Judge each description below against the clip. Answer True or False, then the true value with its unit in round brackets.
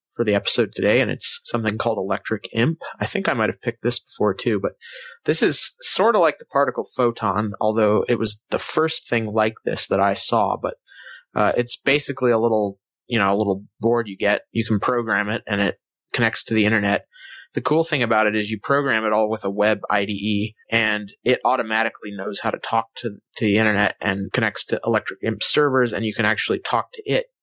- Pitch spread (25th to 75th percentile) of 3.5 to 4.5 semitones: False (2.7 semitones)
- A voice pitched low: True (110 Hz)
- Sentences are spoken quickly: True (220 wpm)